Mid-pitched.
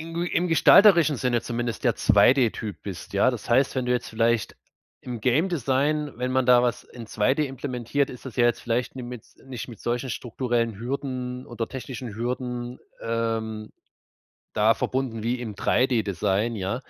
No: low, 125 Hz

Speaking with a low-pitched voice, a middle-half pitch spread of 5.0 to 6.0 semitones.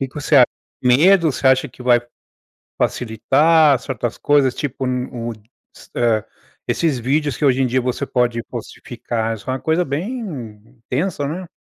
No: low, 130 Hz; average, 3.2 semitones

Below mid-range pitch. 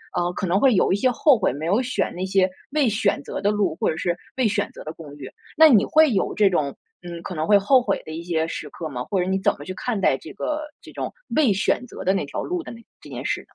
No: high, 195 Hz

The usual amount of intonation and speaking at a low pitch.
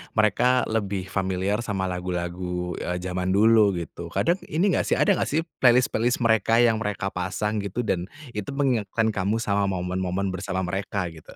Yes: average, 3.5 semitones; low, 100 Hz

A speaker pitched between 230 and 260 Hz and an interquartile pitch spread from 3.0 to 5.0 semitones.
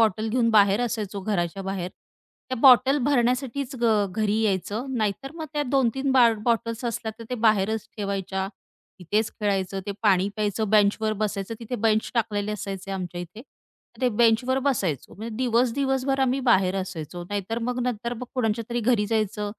No: high, 220 Hz; average, 3.6 semitones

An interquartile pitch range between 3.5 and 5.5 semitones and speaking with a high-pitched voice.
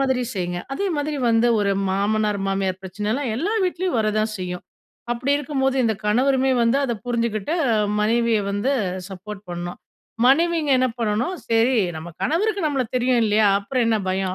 Yes: average, 4.6 semitones; high, 230 Hz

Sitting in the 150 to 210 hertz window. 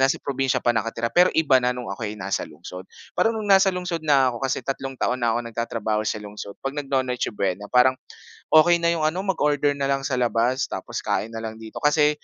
No: low, 130 Hz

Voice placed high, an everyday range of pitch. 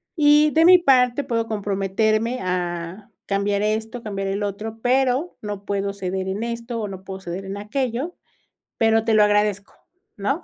Yes: high, 215 Hz; average, 3.6 semitones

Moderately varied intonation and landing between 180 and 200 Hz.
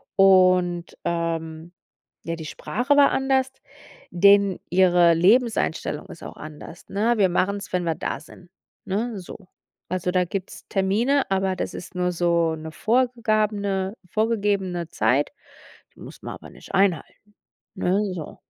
Yes: average, 3.3 semitones; high, 190 Hz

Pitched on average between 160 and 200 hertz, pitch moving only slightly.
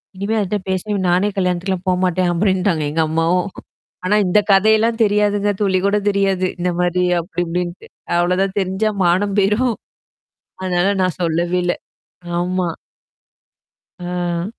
Yes: medium, 185 Hz; narrow, 2.2 semitones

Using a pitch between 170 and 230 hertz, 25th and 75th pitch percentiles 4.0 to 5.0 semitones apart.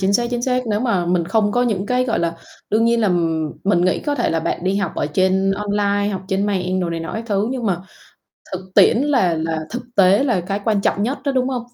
Yes: high, 200 Hz; average, 4.3 semitones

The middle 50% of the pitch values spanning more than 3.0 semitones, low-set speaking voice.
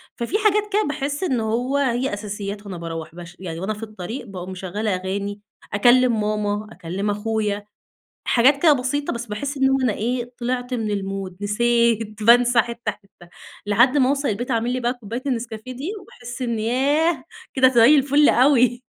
No: average, 3.8 semitones; high, 235 Hz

